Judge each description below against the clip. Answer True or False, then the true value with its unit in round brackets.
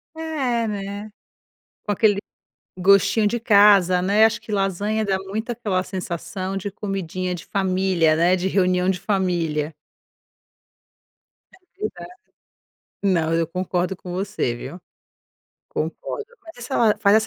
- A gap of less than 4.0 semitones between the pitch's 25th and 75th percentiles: True (2.8 semitones)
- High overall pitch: True (195 Hz)